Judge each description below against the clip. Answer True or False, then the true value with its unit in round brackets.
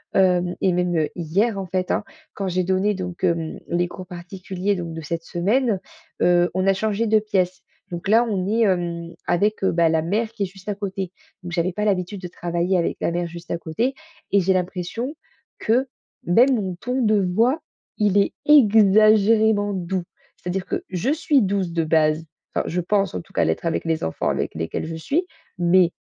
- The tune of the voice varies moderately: True (3.3 semitones)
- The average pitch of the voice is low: False (185 Hz)